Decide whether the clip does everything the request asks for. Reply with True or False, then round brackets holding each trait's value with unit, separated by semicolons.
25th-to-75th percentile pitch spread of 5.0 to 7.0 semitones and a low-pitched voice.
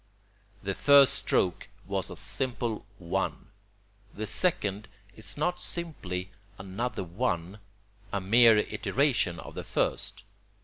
True (5.3 semitones; 105 Hz)